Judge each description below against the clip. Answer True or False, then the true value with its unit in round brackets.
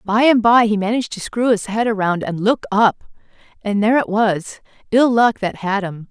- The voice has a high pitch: True (215 Hz)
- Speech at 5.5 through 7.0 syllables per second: False (5.0 syllables/s)